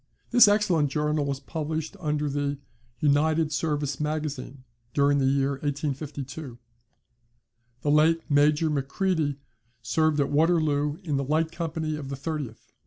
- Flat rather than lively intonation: Yes, narrow, 1.9 semitones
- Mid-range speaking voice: Yes, medium, 150 Hz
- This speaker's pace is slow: Yes, slow, 130 wpm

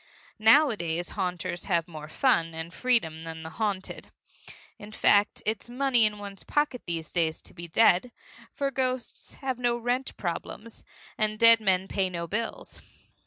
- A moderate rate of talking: Yes, average, 155 wpm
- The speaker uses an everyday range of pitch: No, wide, 5.9 semitones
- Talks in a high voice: Yes, high, 205 Hz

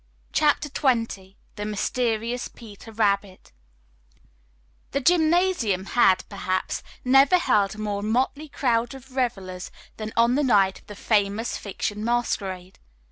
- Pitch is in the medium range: No, high, 225 Hz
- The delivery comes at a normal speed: No, slow, 125 wpm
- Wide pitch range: No, average, 4.3 semitones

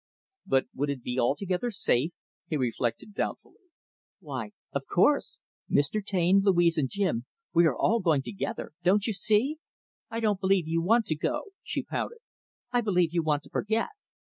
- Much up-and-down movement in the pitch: Yes, wide, 6.1 semitones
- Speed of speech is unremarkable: Yes, average, 165 wpm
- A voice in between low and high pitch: Yes, medium, 175 Hz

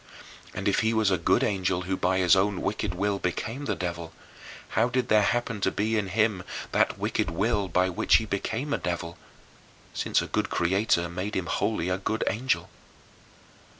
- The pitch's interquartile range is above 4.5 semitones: No, average, 3.3 semitones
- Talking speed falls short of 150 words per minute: No, average, 185 wpm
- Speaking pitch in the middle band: No, low, 100 Hz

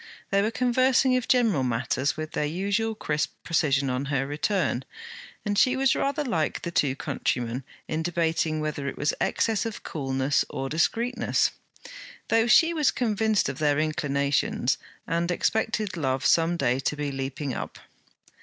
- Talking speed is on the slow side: No, average, 155 wpm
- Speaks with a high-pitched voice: No, medium, 160 Hz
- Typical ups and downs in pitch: No, wide, 7.9 semitones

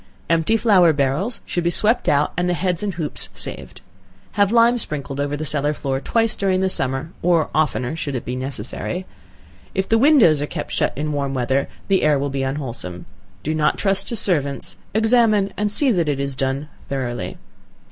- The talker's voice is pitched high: No, medium, 155 Hz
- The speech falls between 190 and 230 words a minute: Yes, average, 195 wpm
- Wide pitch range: Yes, wide, 6.1 semitones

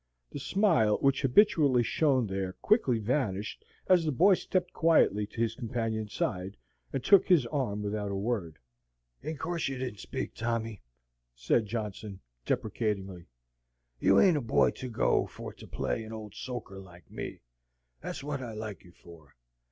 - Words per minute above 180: No, average, 160 wpm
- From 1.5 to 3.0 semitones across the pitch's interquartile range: No, average, 5.2 semitones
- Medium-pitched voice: No, low, 115 Hz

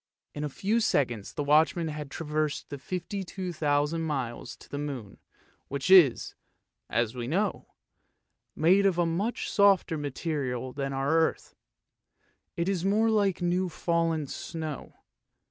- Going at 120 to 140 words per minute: Yes, slow, 135 wpm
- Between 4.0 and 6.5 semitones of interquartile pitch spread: Yes, average, 4.3 semitones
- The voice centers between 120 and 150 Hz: No, medium, 160 Hz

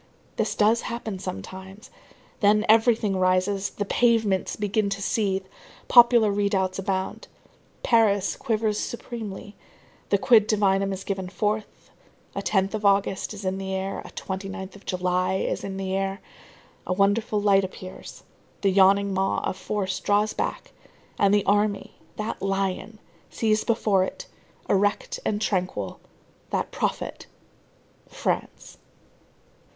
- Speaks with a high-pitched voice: Yes, high, 200 Hz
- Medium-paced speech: No, slow, 130 wpm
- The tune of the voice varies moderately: No, narrow, 1.9 semitones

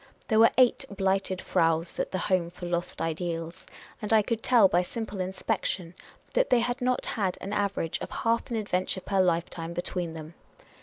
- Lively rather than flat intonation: No, average, 4.1 semitones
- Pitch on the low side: No, high, 190 Hz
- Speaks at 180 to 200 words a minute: Yes, average, 185 wpm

